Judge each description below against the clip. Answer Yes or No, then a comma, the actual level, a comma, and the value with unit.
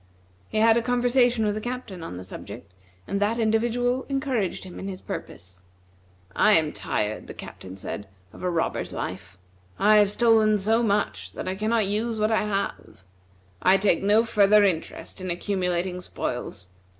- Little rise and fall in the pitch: No, average, 3.9 semitones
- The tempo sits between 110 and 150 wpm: No, average, 170 wpm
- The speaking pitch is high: Yes, high, 205 Hz